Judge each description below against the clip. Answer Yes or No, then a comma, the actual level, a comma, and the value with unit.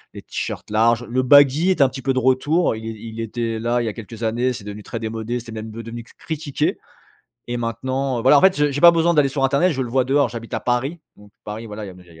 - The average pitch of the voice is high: No, low, 120 Hz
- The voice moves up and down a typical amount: Yes, average, 3.5 semitones